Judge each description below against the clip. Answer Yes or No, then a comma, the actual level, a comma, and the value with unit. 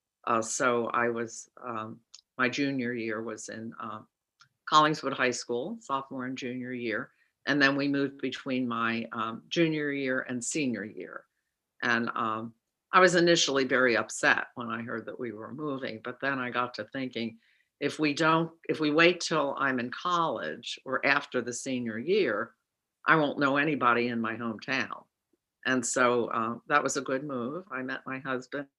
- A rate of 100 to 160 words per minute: No, average, 175 wpm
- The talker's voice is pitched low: Yes, low, 130 Hz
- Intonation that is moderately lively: Yes, average, 3.0 semitones